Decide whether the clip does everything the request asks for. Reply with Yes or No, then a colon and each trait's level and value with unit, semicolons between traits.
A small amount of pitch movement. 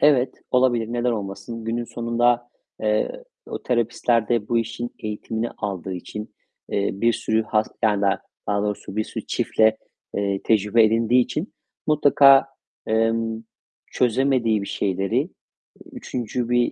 Yes: narrow, 2.3 semitones